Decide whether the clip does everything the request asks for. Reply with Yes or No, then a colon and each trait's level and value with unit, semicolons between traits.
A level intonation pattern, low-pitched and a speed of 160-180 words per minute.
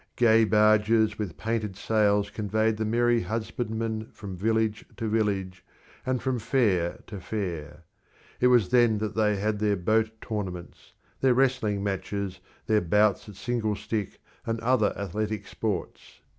No: narrow, 2.0 semitones; low, 110 Hz; average, 145 wpm